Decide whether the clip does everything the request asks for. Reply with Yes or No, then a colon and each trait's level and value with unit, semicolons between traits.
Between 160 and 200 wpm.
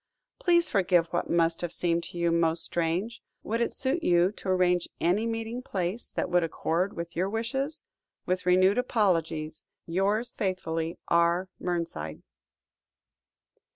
No: average, 140 wpm